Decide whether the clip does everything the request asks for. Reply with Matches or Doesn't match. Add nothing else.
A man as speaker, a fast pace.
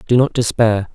Doesn't match